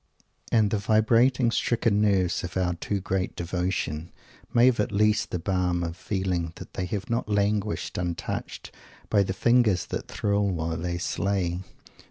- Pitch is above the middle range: No, very low, 95 Hz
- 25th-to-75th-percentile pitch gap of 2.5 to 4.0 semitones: Yes, average, 3.2 semitones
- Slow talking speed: No, average, 165 wpm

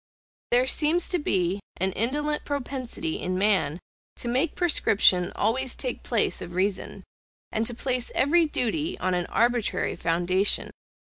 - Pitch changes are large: Yes, wide, 7.1 semitones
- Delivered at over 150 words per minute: No, average, 140 wpm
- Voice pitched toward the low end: No, high, 235 Hz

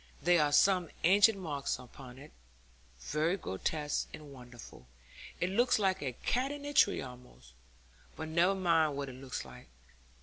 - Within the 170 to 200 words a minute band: No, average, 160 wpm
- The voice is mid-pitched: Yes, medium, 155 Hz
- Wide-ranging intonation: Yes, wide, 6.5 semitones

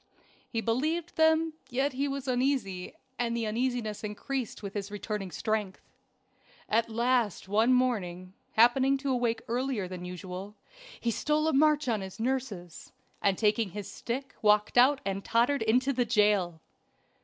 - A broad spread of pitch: No, average, 4.2 semitones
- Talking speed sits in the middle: Yes, average, 150 wpm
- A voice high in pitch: Yes, high, 230 Hz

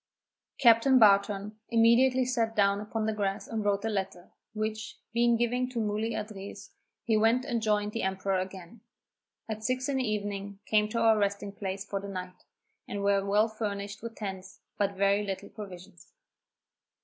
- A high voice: Yes, high, 210 Hz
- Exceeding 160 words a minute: Yes, average, 170 wpm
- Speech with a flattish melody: Yes, narrow, 2.3 semitones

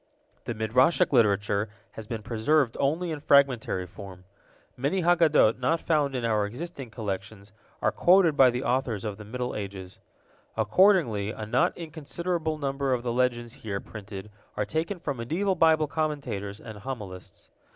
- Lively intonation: Yes, wide, 6.6 semitones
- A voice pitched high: No, low, 125 Hz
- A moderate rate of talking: Yes, average, 150 wpm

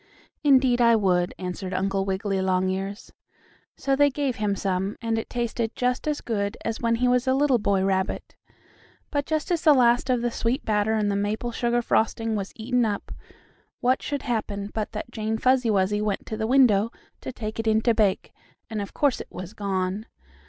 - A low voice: No, high, 220 Hz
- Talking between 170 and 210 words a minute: Yes, average, 195 wpm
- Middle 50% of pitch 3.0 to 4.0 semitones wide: Yes, average, 3.7 semitones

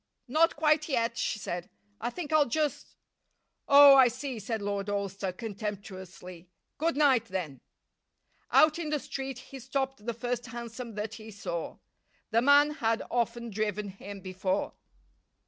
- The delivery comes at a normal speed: Yes, average, 150 wpm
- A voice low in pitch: No, high, 230 Hz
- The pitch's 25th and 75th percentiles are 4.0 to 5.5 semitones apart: Yes, average, 5.2 semitones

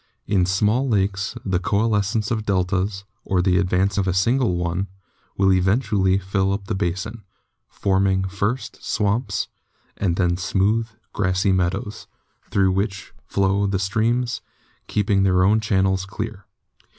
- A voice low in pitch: Yes, low, 100 Hz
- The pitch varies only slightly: Yes, narrow, 2.0 semitones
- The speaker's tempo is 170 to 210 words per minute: No, slow, 135 wpm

